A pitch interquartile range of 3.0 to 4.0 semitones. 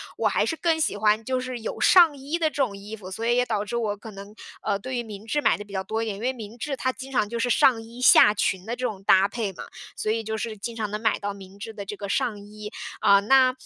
Yes: average, 3.6 semitones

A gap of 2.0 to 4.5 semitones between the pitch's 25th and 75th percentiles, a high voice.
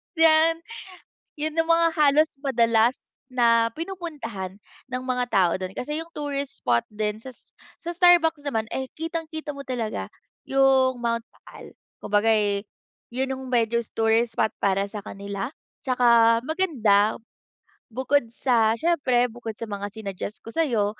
No: average, 5.3 semitones; high, 245 Hz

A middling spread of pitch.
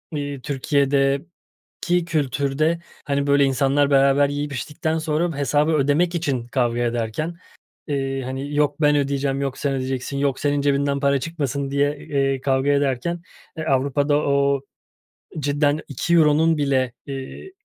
No: narrow, 1.4 semitones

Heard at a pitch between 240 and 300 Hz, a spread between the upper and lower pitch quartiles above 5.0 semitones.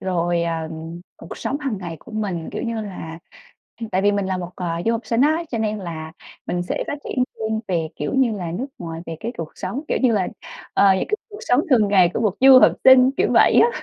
No: high, 200 Hz; wide, 5.5 semitones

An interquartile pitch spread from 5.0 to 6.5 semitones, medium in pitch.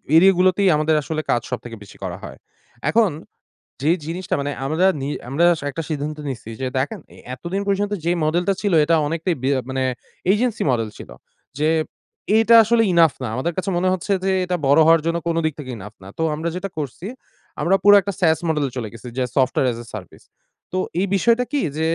Yes: wide, 5.4 semitones; medium, 165 Hz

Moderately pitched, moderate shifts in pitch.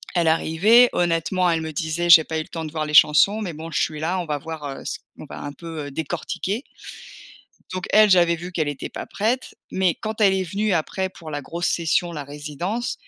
Yes: medium, 165 Hz; average, 3.2 semitones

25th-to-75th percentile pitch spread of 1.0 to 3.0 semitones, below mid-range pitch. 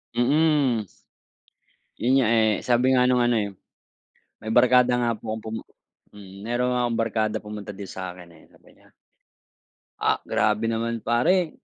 Yes: average, 2.7 semitones; low, 115 Hz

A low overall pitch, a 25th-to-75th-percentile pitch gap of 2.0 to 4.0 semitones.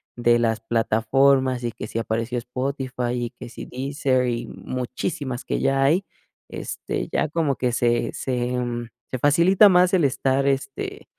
Yes: low, 130 Hz; narrow, 2.6 semitones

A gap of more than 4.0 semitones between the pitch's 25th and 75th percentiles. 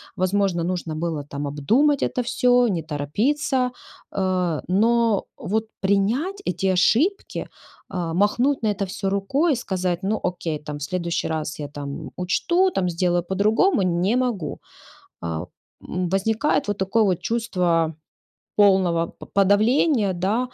Yes: average, 5.0 semitones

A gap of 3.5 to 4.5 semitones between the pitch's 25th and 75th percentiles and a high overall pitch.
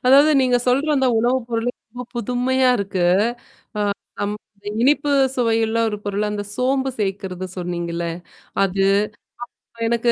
Yes: average, 4.0 semitones; high, 230 Hz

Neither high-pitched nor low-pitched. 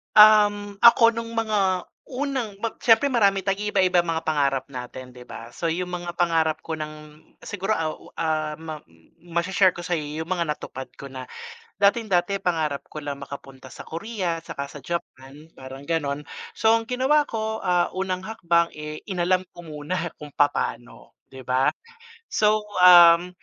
Yes: medium, 170 Hz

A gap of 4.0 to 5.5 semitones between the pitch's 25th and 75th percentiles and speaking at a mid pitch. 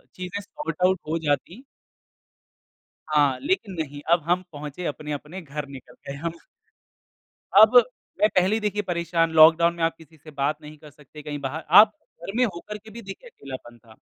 Yes: average, 4.8 semitones; medium, 165 Hz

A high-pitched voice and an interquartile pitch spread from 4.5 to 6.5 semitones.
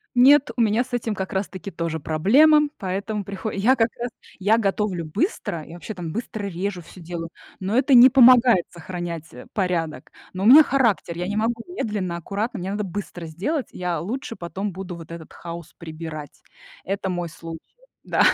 Yes: high, 195 Hz; average, 5.0 semitones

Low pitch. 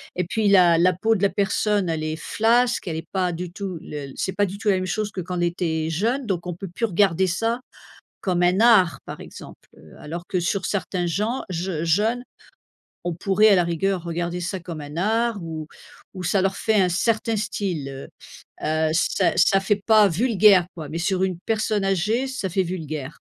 No: medium, 185 Hz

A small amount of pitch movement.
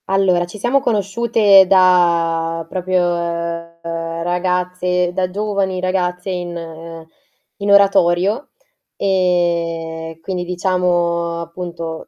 Yes: narrow, 2.0 semitones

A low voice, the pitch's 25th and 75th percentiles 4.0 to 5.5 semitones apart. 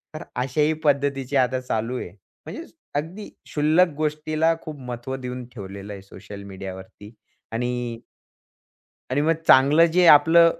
Yes: low, 130 Hz; average, 4.9 semitones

